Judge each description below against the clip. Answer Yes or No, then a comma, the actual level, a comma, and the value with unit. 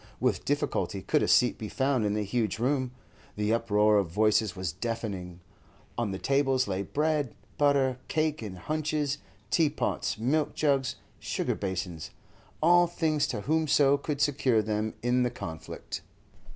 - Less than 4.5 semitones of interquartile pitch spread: No, wide, 5.6 semitones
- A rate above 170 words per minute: No, average, 150 wpm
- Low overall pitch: Yes, low, 125 Hz